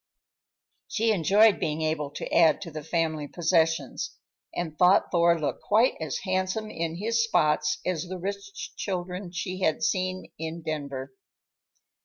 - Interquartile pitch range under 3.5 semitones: Yes, average, 3.1 semitones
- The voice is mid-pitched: Yes, medium, 170 Hz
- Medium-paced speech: Yes, average, 145 wpm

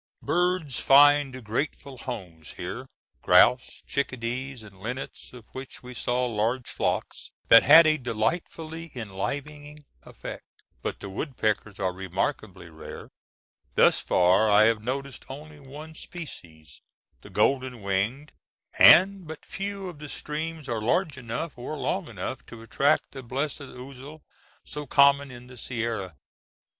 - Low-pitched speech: Yes, low, 130 Hz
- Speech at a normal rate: No, slow, 130 wpm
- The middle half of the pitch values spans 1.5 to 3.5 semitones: No, average, 5.0 semitones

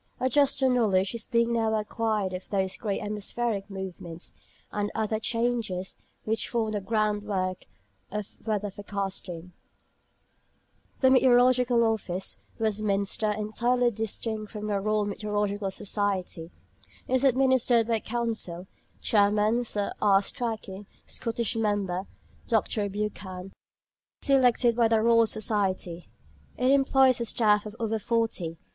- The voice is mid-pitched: No, high, 215 Hz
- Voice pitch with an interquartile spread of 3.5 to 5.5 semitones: No, average, 2.8 semitones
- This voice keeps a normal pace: No, slow, 120 wpm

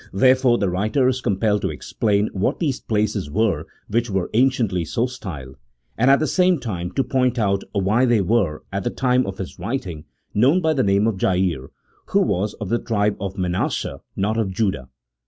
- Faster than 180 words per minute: Yes, average, 195 wpm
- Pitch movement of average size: Yes, average, 4.9 semitones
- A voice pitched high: No, low, 105 Hz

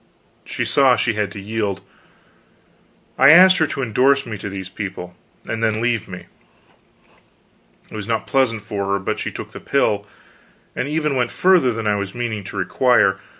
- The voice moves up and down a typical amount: Yes, average, 4.6 semitones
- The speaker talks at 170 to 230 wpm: Yes, average, 180 wpm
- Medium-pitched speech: No, low, 110 Hz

